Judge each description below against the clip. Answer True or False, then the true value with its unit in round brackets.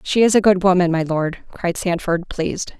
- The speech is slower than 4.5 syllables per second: False (5.0 syllables/s)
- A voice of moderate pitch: True (180 Hz)